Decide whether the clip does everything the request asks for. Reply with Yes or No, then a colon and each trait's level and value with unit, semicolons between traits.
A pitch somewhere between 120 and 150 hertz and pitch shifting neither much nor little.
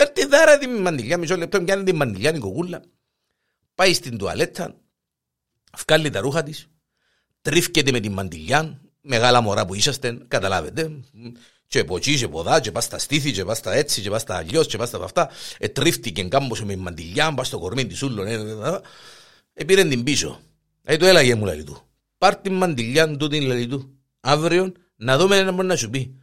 No: medium, 140 Hz; wide, 6.3 semitones